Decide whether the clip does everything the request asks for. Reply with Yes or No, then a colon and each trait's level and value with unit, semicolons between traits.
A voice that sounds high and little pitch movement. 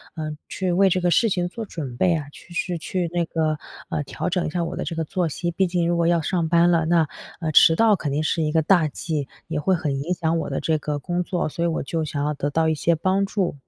No: medium, 170 Hz; narrow, 2.3 semitones